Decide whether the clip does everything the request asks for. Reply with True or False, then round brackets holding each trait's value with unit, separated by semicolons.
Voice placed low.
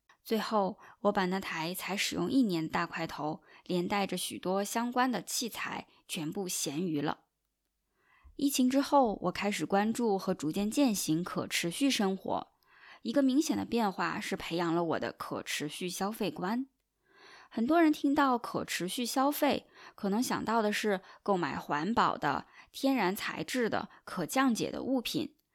False (205 Hz)